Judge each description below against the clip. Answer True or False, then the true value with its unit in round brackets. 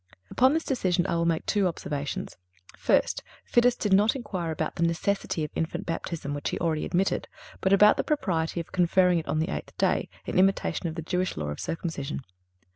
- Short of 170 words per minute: False (195 wpm)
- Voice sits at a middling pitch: True (170 Hz)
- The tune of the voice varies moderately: True (3.3 semitones)